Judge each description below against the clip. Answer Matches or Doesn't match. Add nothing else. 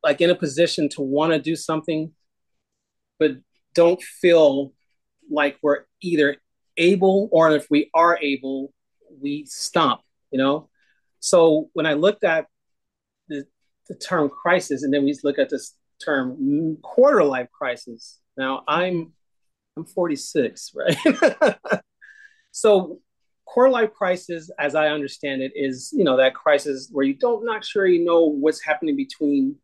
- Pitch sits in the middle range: Matches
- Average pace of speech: Matches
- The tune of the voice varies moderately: Matches